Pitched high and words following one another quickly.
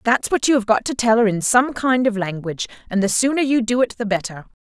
Yes: high, 230 Hz; fast, 270 wpm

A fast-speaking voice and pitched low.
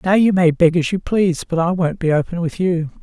No: fast, 280 wpm; medium, 175 Hz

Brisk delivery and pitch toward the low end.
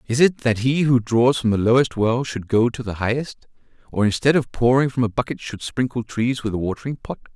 Yes: fast, 235 wpm; low, 120 Hz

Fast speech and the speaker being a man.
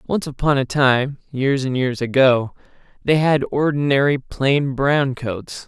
No: average, 150 wpm; male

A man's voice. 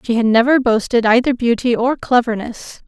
No: female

